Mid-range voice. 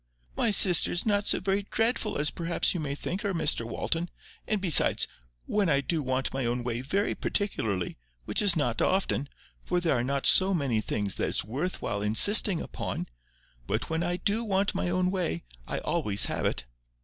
Yes: medium, 165 Hz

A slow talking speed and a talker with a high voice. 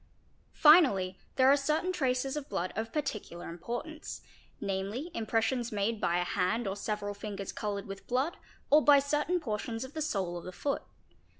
No: average, 170 wpm; high, 225 Hz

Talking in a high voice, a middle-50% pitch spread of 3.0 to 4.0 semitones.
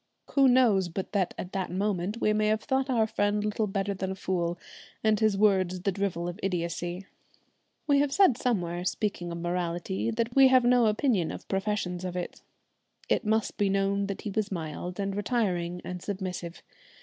Yes: high, 195 Hz; average, 3.4 semitones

